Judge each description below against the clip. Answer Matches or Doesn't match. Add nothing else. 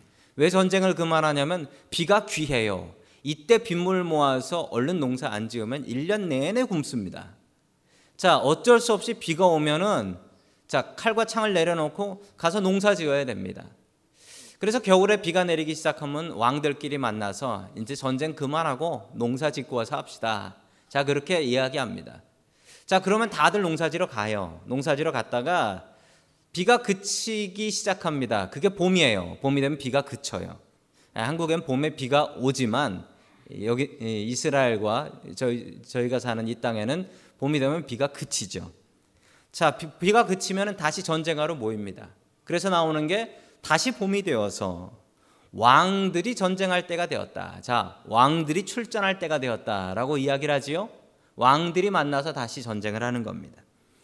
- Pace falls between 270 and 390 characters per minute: Matches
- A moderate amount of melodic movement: Doesn't match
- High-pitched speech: Doesn't match